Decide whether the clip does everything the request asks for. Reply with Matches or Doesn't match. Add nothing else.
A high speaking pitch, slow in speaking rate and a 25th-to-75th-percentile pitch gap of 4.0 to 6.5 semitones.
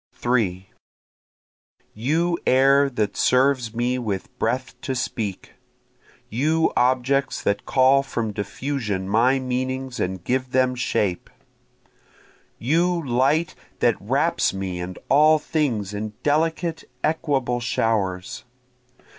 Doesn't match